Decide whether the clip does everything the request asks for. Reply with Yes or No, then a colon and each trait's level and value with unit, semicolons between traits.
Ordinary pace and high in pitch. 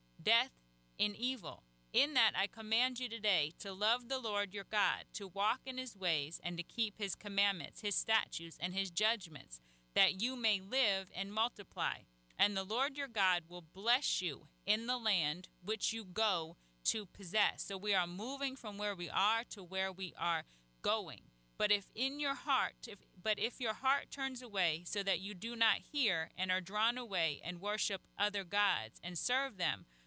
Yes: average, 190 wpm; high, 205 Hz